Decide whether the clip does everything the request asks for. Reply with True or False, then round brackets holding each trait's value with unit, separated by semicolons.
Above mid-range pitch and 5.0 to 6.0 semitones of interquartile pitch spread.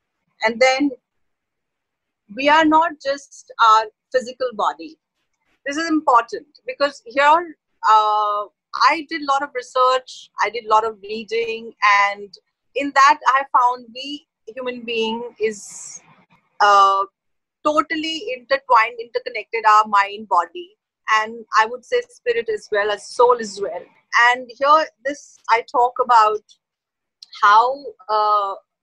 True (250 Hz; 5.6 semitones)